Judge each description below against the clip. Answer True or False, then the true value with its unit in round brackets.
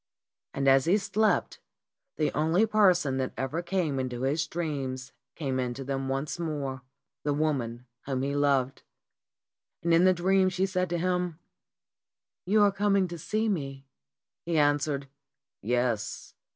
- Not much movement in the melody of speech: False (5.1 semitones)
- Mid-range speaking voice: True (150 Hz)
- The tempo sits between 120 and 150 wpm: True (145 wpm)